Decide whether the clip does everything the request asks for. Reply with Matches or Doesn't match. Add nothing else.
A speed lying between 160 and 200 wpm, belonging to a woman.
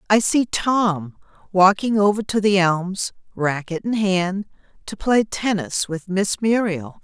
Doesn't match